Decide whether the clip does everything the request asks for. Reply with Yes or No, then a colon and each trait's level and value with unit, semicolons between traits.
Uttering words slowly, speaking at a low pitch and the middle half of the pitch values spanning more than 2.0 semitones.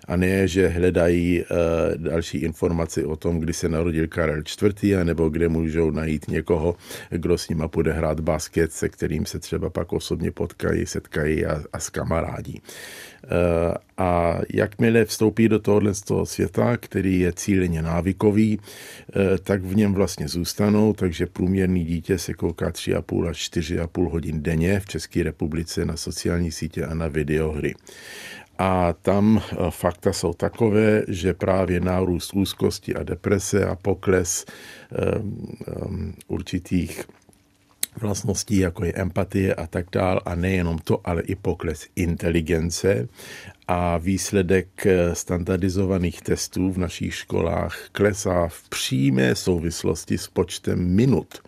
No: average, 140 wpm; very low, 90 Hz; narrow, 2.6 semitones